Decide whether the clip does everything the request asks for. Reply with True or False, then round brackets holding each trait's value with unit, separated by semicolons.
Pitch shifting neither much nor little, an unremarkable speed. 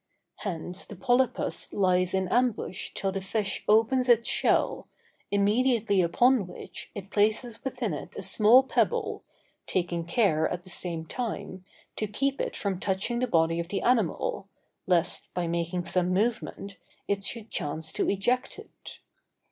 True (4.8 semitones; 150 wpm)